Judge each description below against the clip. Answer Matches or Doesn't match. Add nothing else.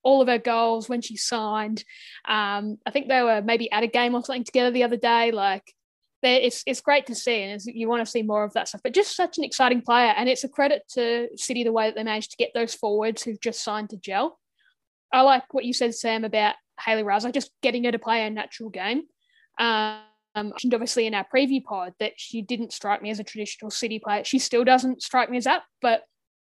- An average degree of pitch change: Matches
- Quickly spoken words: Matches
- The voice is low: Doesn't match